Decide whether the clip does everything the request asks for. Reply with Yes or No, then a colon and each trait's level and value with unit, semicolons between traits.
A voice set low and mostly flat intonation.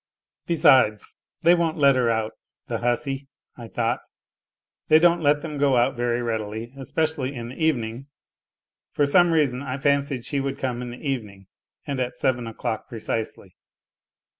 No: low, 130 Hz; average, 3.3 semitones